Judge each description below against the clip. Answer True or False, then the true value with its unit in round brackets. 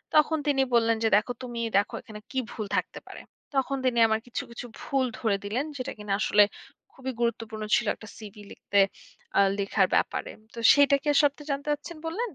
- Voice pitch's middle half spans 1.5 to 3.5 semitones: False (4.4 semitones)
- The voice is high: True (240 Hz)